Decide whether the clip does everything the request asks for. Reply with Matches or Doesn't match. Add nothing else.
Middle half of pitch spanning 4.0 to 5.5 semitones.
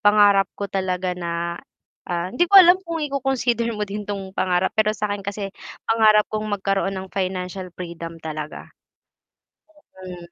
Doesn't match